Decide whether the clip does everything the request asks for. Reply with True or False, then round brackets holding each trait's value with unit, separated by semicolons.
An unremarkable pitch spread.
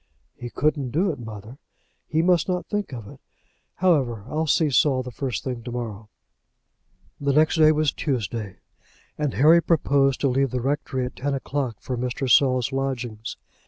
True (3.8 semitones)